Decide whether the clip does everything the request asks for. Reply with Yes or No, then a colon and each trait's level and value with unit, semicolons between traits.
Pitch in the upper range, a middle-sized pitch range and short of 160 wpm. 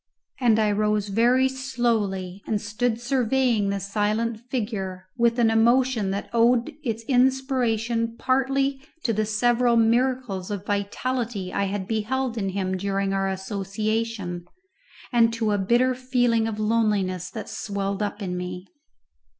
Yes: high, 225 Hz; average, 3.4 semitones; average, 140 wpm